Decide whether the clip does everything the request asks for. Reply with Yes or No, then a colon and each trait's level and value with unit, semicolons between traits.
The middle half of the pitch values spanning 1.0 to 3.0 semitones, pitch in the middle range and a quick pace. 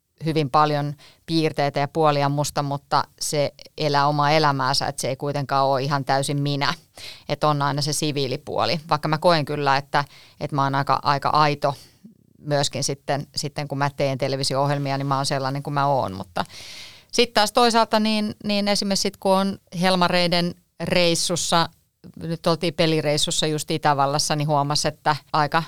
Yes: average, 2.7 semitones; medium, 145 Hz; fast, 165 wpm